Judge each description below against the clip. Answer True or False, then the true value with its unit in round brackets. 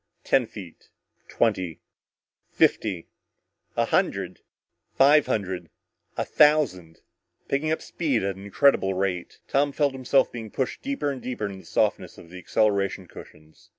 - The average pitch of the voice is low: True (110 Hz)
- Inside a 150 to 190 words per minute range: False (140 wpm)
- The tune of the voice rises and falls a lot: True (6.8 semitones)